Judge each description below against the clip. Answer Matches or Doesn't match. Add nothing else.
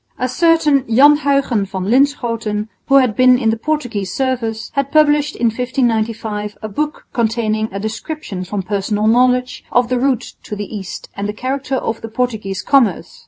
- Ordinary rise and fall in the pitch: Matches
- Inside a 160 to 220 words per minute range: Matches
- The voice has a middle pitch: Doesn't match